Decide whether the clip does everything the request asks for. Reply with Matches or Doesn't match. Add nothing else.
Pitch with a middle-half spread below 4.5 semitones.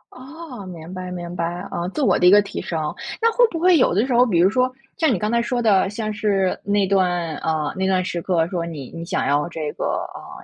Doesn't match